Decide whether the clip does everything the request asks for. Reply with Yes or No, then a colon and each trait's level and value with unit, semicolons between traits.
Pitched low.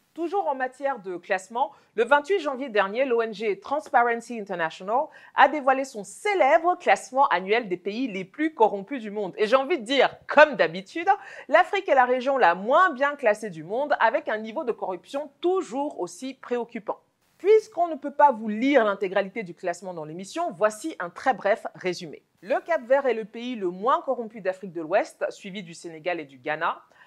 No: high, 245 Hz